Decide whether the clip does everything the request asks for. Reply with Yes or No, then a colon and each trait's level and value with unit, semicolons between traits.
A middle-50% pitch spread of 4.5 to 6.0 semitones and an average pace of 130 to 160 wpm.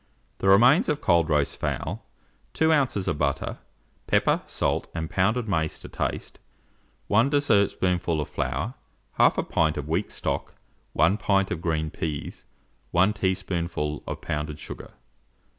Yes: average, 4.9 semitones; average, 140 wpm